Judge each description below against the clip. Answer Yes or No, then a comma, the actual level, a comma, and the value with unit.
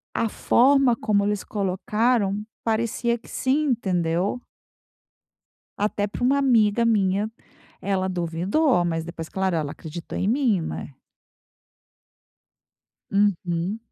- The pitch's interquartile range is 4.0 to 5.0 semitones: Yes, average, 4.4 semitones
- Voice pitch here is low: No, high, 205 Hz